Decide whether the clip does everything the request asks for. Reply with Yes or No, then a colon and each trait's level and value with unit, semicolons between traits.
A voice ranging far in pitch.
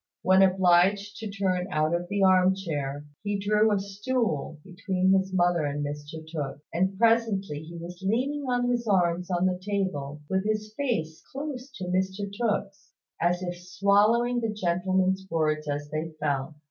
No: average, 3.3 semitones